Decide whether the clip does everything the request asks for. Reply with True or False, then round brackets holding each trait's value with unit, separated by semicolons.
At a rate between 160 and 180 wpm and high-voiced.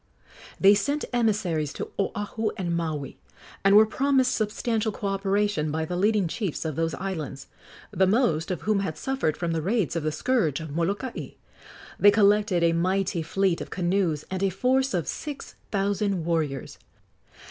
True (165 wpm; 195 Hz)